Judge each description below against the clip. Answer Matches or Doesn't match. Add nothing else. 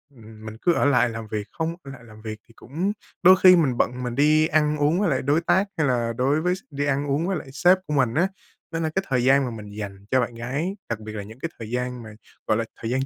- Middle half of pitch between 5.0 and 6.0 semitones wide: Matches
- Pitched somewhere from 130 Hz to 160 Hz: Matches